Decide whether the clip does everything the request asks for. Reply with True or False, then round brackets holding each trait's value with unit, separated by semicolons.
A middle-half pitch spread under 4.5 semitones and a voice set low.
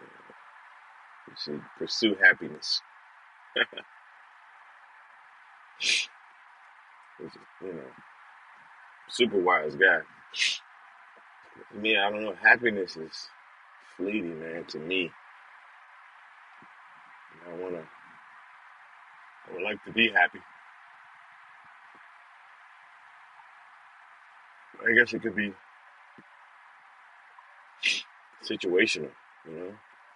False (4.8 semitones; 100 Hz)